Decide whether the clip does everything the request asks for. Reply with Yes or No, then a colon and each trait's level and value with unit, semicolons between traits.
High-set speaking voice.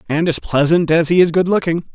No: medium, 165 Hz